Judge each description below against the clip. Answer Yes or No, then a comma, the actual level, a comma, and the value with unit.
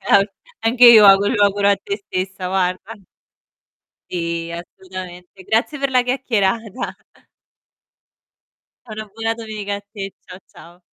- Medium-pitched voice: No, high, 200 Hz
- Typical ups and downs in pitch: Yes, average, 3.3 semitones